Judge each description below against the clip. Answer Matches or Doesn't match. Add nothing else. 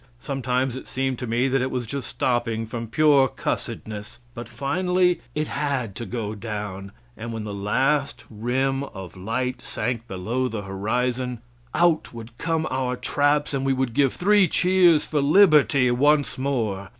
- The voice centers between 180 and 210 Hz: Doesn't match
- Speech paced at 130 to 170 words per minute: Matches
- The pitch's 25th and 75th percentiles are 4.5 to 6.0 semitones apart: Doesn't match